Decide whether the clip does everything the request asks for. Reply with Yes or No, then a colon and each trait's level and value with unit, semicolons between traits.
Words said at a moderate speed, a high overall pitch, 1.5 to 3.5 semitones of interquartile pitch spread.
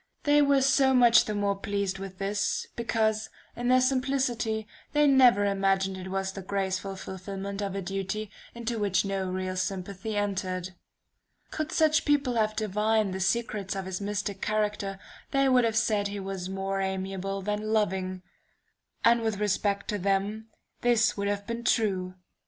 Yes: average, 165 wpm; high, 205 Hz; average, 2.9 semitones